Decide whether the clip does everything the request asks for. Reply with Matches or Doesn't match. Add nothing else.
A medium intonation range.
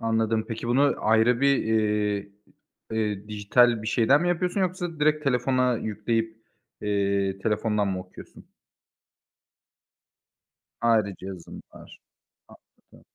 Matches